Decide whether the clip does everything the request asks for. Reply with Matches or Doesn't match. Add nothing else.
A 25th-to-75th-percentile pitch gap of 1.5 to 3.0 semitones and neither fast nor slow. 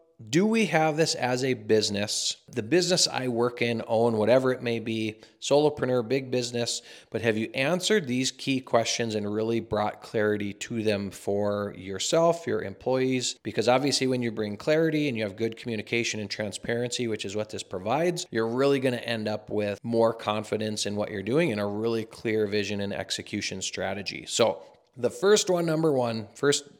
Doesn't match